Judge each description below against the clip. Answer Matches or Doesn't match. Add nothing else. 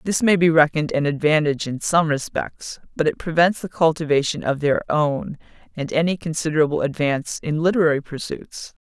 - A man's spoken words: Doesn't match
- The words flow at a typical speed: Matches